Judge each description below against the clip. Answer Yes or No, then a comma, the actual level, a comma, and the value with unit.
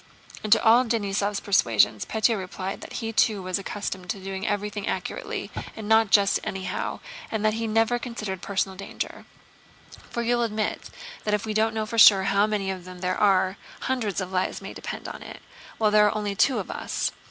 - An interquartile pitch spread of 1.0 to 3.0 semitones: Yes, narrow, 2.5 semitones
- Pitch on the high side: Yes, high, 205 Hz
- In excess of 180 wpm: Yes, average, 200 wpm